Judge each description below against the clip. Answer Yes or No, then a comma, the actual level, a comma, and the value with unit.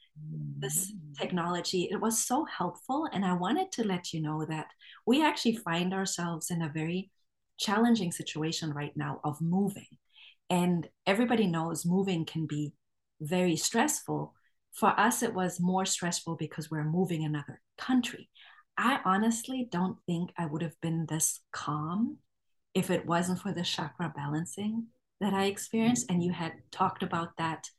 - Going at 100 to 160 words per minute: Yes, average, 155 wpm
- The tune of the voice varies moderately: Yes, average, 3.8 semitones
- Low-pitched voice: No, medium, 175 Hz